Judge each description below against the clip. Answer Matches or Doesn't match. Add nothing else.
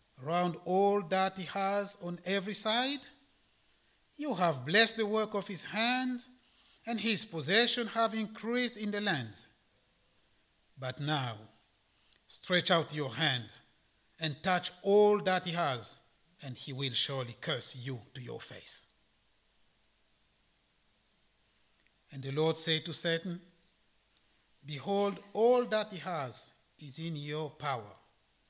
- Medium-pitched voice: Matches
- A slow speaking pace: Matches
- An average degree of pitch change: Doesn't match